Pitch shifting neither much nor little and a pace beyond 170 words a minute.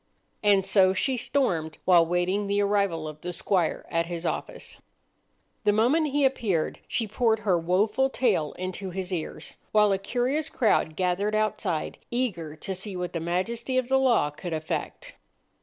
No: average, 4.7 semitones; average, 165 wpm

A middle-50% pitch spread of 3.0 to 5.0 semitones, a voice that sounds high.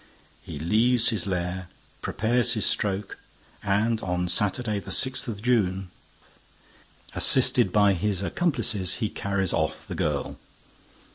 No: average, 3.6 semitones; low, 100 Hz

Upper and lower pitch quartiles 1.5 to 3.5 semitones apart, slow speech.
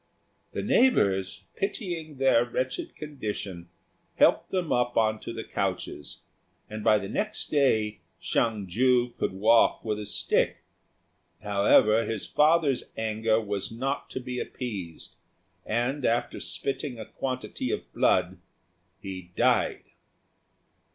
No: average, 4.3 semitones; slow, 125 wpm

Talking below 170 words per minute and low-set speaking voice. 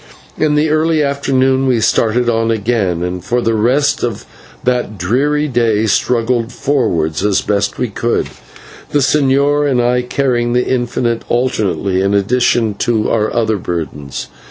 Yes: average, 150 wpm; low, 120 Hz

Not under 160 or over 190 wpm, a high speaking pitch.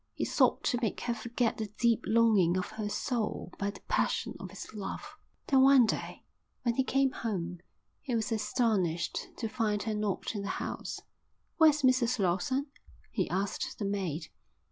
Yes: average, 170 wpm; high, 220 Hz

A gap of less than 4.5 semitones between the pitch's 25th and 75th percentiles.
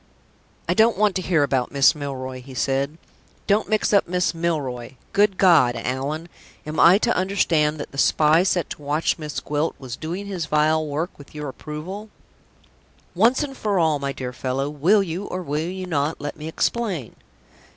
No: average, 4.8 semitones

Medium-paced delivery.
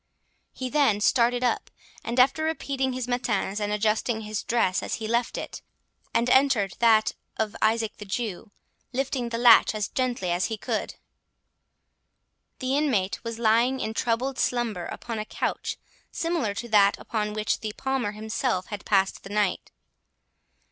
Yes: average, 155 wpm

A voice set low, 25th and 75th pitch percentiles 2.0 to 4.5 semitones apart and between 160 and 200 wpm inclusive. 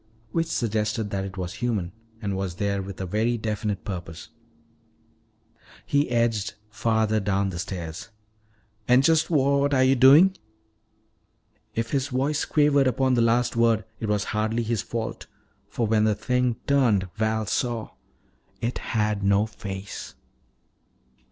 No: low, 110 Hz; average, 3.8 semitones; average, 140 wpm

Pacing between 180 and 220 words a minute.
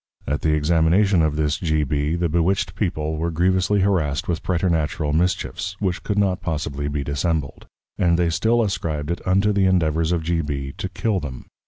Yes: average, 185 wpm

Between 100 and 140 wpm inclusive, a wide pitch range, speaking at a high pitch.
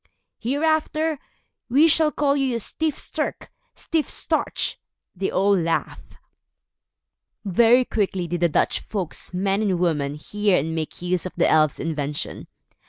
Yes: slow, 135 wpm; wide, 8.1 semitones; high, 195 Hz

